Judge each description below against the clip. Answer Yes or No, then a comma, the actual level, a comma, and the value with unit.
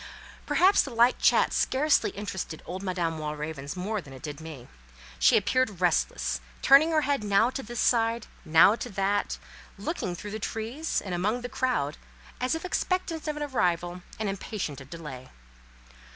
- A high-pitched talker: Yes, high, 200 Hz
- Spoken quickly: No, average, 165 wpm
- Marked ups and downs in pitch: Yes, wide, 7.5 semitones